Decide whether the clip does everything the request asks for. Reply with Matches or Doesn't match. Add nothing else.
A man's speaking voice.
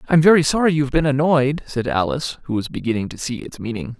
Matches